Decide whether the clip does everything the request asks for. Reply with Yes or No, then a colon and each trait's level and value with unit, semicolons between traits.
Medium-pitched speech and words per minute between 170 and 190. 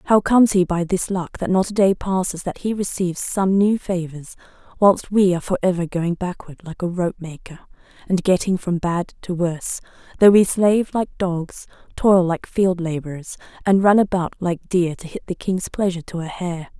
No: medium, 180 Hz; average, 200 wpm